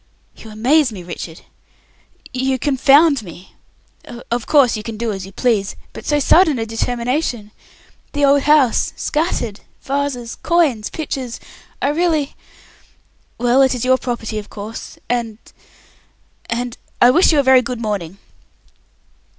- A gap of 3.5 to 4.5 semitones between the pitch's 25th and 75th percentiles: Yes, average, 4.2 semitones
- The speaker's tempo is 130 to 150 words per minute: Yes, average, 140 wpm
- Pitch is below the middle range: No, high, 245 Hz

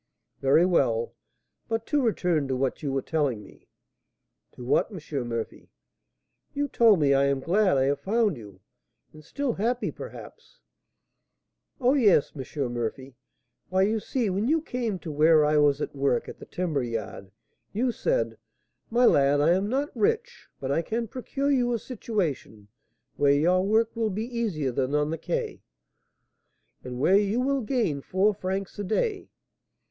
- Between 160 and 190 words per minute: Yes, average, 170 wpm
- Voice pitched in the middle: Yes, medium, 180 Hz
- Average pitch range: No, wide, 8.7 semitones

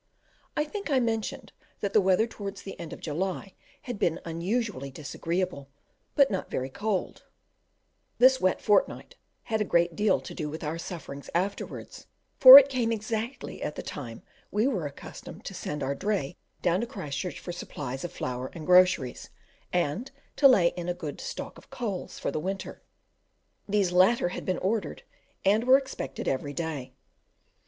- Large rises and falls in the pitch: Yes, wide, 5.7 semitones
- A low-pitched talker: No, medium, 185 Hz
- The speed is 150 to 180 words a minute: Yes, average, 170 wpm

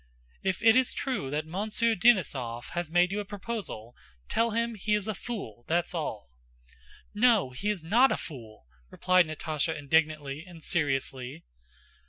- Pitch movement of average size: No, wide, 6.7 semitones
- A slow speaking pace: No, average, 150 wpm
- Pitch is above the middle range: No, medium, 175 Hz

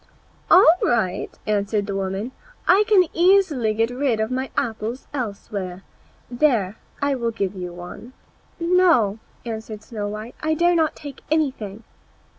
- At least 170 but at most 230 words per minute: No, average, 140 wpm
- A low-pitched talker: No, high, 230 Hz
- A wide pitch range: Yes, wide, 6.4 semitones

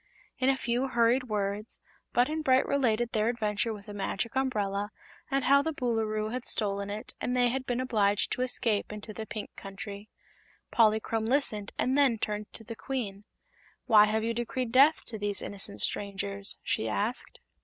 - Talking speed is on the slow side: No, average, 175 wpm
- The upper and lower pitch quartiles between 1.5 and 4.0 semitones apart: Yes, average, 3.5 semitones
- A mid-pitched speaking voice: No, high, 225 Hz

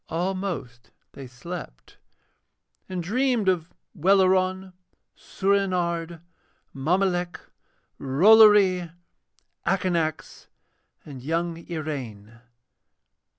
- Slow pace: Yes, slow, 65 wpm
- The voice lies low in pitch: No, medium, 175 Hz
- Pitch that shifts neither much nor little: Yes, average, 3.6 semitones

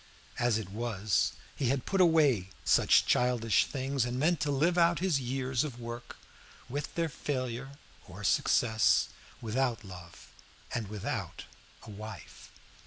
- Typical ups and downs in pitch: Yes, average, 4.3 semitones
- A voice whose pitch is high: No, low, 125 Hz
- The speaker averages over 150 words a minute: No, average, 140 wpm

